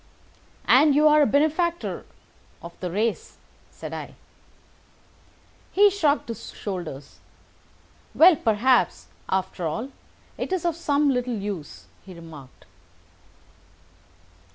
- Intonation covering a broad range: Yes, wide, 8.4 semitones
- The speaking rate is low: Yes, slow, 105 wpm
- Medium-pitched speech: No, very high, 250 Hz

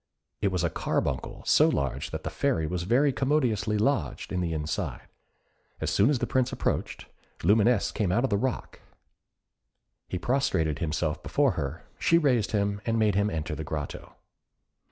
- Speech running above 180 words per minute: No, average, 170 wpm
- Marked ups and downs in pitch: Yes, wide, 7.2 semitones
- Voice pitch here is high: No, low, 100 Hz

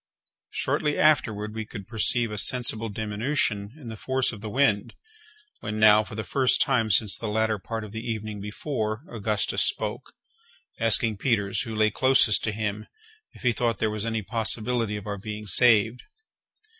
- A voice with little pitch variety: Yes, narrow, 1.9 semitones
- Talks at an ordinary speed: Yes, average, 170 wpm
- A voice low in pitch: Yes, low, 110 Hz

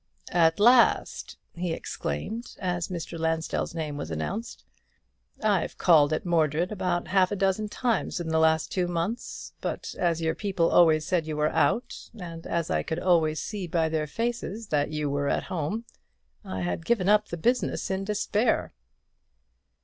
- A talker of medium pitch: Yes, medium, 170 Hz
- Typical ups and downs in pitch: Yes, average, 4.0 semitones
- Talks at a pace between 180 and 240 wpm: No, average, 165 wpm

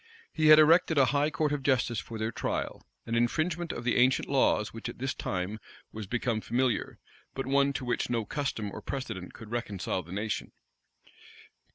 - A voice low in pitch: Yes, low, 120 Hz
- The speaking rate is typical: Yes, average, 185 wpm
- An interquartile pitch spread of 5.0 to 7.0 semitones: No, average, 4.2 semitones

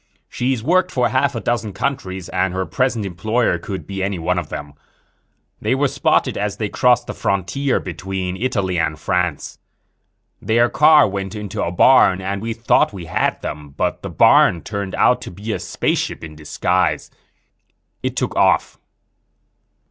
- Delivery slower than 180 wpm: Yes, average, 165 wpm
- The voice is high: No, low, 100 Hz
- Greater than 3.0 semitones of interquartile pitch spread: Yes, average, 4.9 semitones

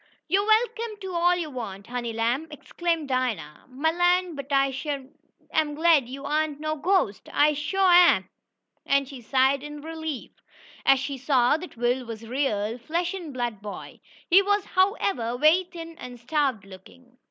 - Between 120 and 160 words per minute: No, average, 175 wpm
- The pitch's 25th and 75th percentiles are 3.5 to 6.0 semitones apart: Yes, wide, 5.6 semitones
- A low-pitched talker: No, very high, 290 Hz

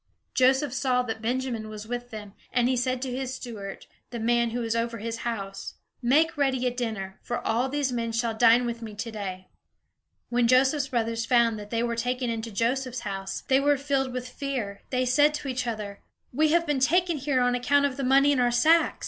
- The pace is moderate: No, fast, 210 wpm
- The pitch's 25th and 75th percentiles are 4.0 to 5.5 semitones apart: No, narrow, 2.6 semitones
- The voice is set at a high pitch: Yes, high, 245 Hz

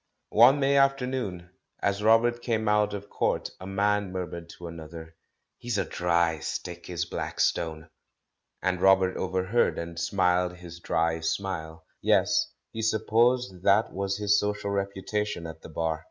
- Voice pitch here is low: Yes, very low, 95 Hz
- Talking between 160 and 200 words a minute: No, average, 145 wpm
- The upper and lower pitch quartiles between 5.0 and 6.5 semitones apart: No, average, 3.6 semitones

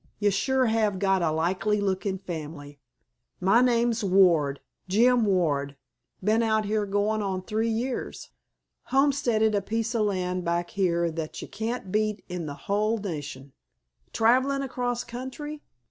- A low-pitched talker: No, high, 205 Hz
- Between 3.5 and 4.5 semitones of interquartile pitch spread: Yes, average, 4.2 semitones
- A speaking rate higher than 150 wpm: No, average, 140 wpm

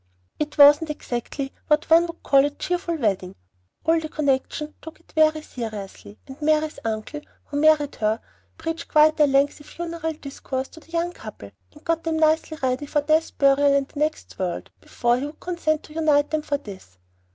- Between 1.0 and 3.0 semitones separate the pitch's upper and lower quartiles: Yes, narrow, 2.6 semitones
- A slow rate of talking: No, average, 185 wpm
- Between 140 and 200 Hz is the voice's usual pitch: No, very high, 300 Hz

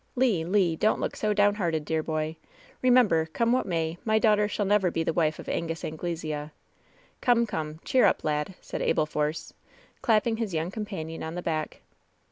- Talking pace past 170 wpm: Yes, average, 200 wpm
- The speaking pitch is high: No, medium, 170 Hz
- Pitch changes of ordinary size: Yes, average, 5.0 semitones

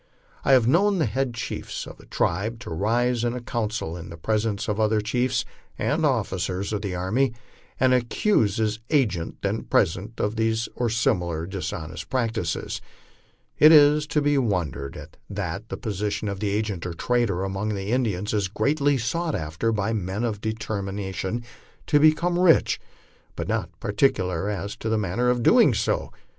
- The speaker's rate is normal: Yes, average, 170 wpm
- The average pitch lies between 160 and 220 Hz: No, low, 110 Hz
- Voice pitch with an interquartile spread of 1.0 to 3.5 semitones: No, average, 4.2 semitones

